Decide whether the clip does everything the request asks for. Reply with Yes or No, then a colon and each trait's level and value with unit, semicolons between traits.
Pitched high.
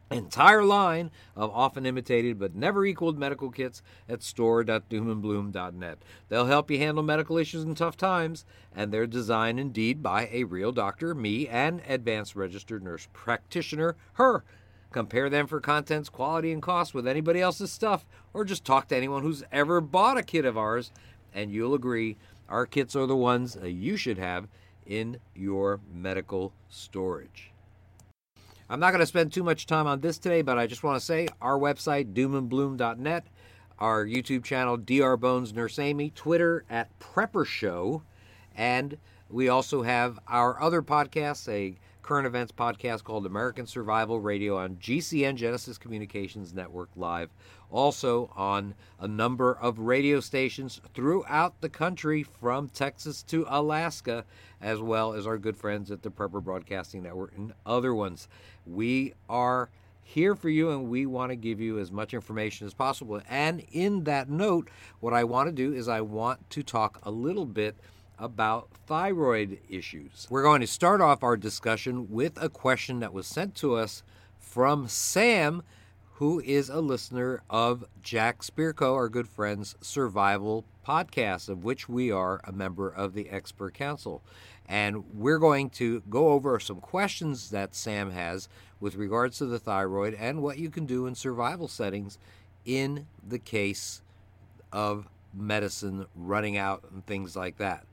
No: low, 115 Hz